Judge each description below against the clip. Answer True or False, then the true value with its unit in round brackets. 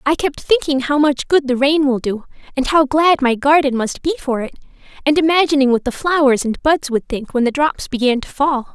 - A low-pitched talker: False (280 Hz)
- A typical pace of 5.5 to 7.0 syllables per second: False (5.3 syllables/s)